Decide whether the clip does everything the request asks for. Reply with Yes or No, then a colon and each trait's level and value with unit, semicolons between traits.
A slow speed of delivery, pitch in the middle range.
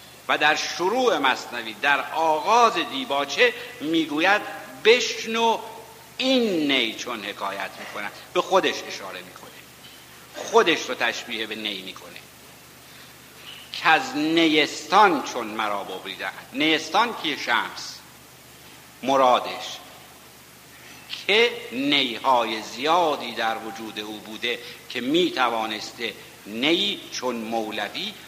Yes: slow, 100 wpm; medium, 150 Hz